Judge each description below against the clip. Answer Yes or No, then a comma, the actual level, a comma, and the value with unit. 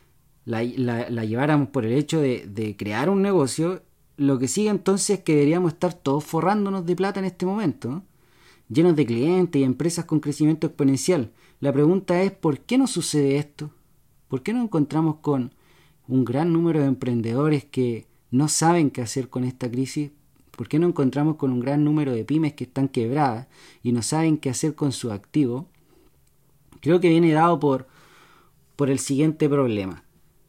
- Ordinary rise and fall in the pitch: Yes, average, 3.9 semitones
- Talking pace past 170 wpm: Yes, average, 180 wpm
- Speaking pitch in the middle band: Yes, medium, 145 Hz